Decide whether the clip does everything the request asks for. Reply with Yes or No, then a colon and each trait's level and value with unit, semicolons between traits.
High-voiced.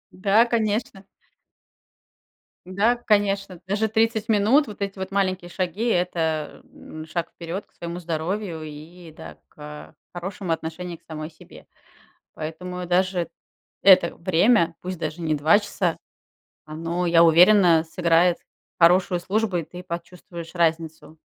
No: medium, 175 Hz